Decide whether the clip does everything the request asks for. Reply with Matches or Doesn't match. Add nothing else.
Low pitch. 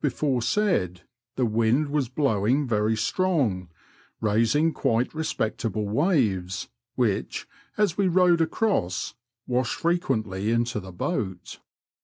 Matches